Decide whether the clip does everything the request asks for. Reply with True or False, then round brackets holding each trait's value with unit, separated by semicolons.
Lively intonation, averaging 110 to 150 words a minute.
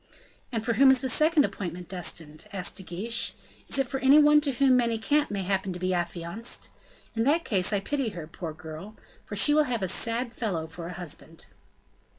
False (6.7 semitones; 200 wpm)